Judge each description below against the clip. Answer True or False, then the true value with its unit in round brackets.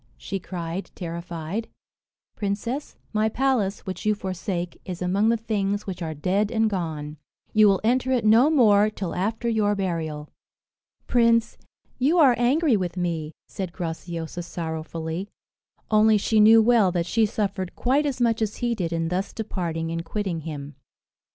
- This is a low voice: False (200 Hz)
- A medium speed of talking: True (155 wpm)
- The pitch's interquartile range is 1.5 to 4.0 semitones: False (4.6 semitones)